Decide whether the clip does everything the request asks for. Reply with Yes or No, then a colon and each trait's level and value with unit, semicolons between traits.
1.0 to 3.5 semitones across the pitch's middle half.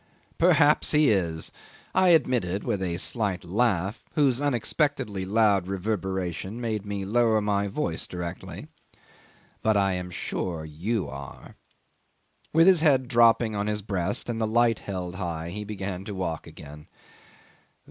No: average, 4.5 semitones